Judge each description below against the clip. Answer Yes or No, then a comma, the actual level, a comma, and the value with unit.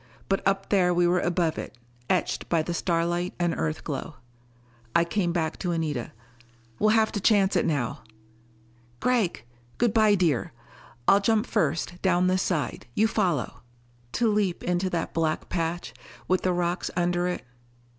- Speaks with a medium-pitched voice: Yes, medium, 175 Hz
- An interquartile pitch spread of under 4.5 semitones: Yes, narrow, 2.5 semitones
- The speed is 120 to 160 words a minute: Yes, average, 155 wpm